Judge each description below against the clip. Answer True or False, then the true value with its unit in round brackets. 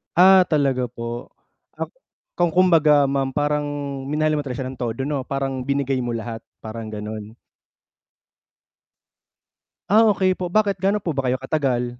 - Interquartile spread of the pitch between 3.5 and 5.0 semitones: True (4.1 semitones)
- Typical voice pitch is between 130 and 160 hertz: True (135 Hz)